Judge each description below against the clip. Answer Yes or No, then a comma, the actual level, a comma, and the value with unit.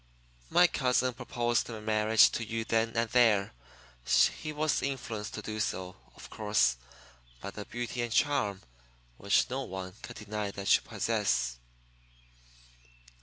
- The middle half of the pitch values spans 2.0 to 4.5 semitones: Yes, average, 2.9 semitones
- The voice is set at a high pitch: No, low, 110 Hz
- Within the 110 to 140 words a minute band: Yes, slow, 135 wpm